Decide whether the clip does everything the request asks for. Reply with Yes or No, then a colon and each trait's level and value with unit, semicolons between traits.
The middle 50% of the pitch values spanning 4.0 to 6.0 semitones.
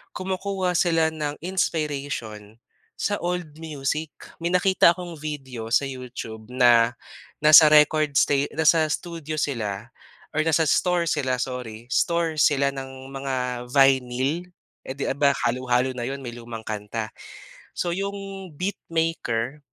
Yes: average, 4.7 semitones